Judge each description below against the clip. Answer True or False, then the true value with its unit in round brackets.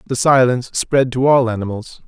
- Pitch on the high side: False (125 Hz)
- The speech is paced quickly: False (175 wpm)